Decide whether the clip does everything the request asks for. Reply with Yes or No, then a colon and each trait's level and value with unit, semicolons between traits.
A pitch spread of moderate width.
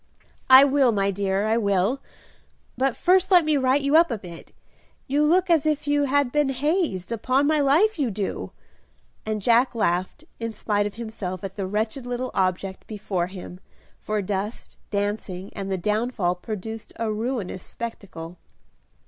No: wide, 5.9 semitones